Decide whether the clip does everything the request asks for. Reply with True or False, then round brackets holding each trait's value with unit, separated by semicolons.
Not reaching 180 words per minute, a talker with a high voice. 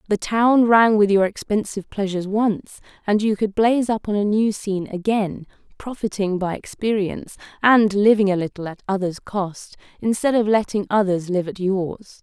True (170 wpm; 205 Hz)